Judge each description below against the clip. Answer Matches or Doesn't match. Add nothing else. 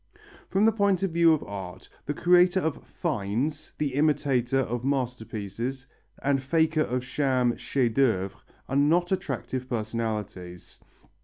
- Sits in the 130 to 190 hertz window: Matches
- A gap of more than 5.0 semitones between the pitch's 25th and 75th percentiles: Matches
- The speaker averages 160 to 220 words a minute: Doesn't match